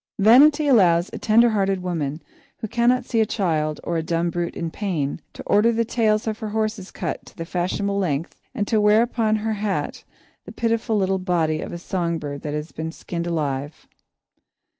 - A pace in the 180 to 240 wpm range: Yes, average, 195 wpm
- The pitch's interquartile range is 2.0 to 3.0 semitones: No, average, 4.7 semitones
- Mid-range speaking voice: No, high, 195 Hz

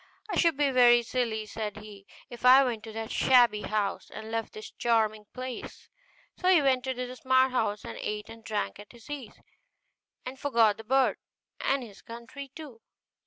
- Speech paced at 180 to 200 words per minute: Yes, average, 185 wpm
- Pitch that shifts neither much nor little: Yes, average, 3.1 semitones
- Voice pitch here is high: Yes, high, 240 Hz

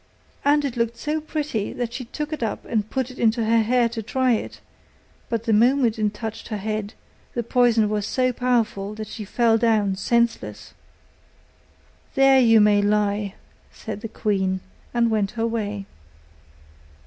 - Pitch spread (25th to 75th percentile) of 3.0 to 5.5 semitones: No, narrow, 2.6 semitones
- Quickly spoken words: No, average, 165 wpm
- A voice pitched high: Yes, high, 225 Hz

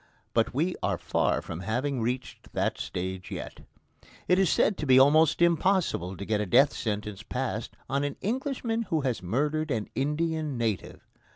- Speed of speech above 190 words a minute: No, average, 170 wpm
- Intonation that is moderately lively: No, wide, 6.5 semitones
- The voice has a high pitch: No, low, 135 Hz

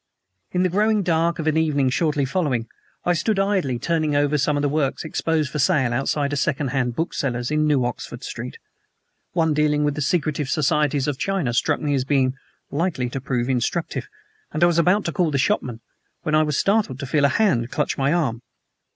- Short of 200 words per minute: No, fast, 205 wpm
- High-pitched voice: No, medium, 150 Hz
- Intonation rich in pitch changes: No, average, 3.7 semitones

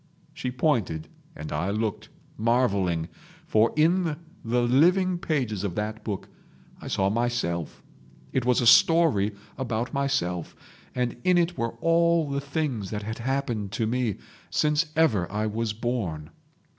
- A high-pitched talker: No, low, 120 Hz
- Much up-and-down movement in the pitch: Yes, wide, 5.7 semitones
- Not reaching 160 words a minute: Yes, average, 145 wpm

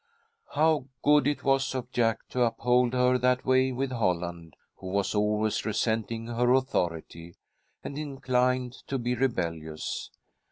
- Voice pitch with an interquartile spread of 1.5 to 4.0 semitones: Yes, average, 3.7 semitones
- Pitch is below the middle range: Yes, low, 125 Hz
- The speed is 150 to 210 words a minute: No, slow, 135 wpm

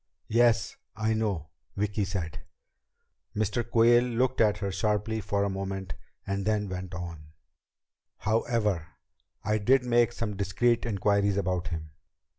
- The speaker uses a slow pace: Yes, slow, 130 wpm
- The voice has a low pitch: Yes, low, 105 Hz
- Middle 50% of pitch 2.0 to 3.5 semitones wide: Yes, average, 2.9 semitones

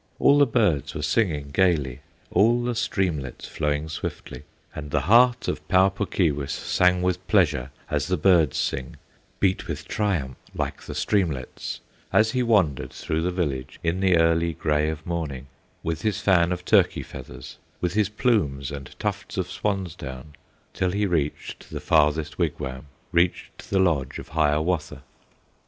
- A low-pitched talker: Yes, very low, 85 Hz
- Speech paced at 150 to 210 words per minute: Yes, average, 160 wpm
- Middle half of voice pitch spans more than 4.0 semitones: Yes, average, 4.7 semitones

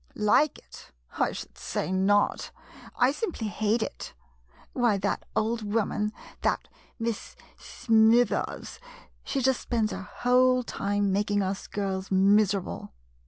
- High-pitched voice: Yes, high, 210 Hz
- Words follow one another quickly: No, slow, 135 wpm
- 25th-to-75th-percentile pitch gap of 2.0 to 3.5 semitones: Yes, average, 3.1 semitones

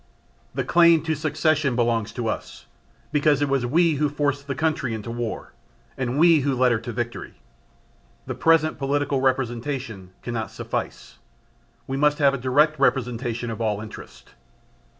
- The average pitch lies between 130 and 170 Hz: Yes, low, 135 Hz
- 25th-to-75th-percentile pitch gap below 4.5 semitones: Yes, average, 3.9 semitones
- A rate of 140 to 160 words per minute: Yes, average, 155 wpm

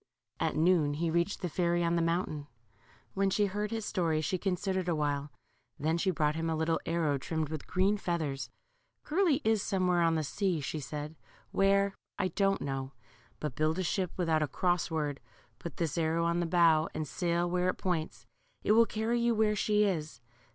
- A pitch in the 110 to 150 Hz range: No, medium, 170 Hz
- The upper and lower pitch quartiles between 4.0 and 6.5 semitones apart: No, average, 3.6 semitones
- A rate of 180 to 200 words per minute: Yes, average, 195 wpm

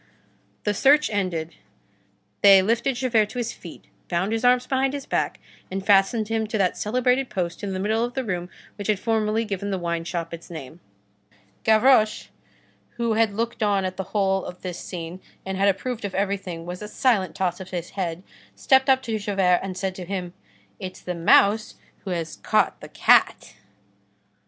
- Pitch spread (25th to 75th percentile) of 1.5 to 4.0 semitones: Yes, average, 3.7 semitones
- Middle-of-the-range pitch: No, high, 200 Hz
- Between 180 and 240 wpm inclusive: Yes, average, 185 wpm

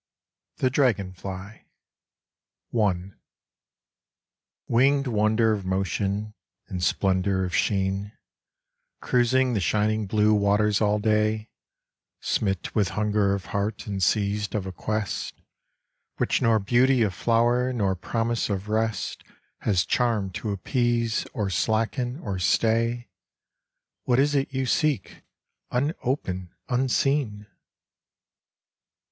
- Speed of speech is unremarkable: No, slow, 105 wpm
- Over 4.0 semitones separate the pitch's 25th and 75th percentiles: No, average, 3.3 semitones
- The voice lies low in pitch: Yes, low, 105 Hz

